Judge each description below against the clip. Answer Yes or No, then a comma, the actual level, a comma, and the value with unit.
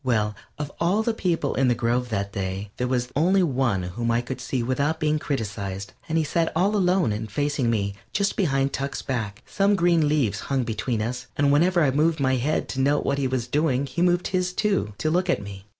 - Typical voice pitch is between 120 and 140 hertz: Yes, low, 135 Hz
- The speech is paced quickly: Yes, fast, 225 wpm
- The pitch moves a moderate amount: No, wide, 5.8 semitones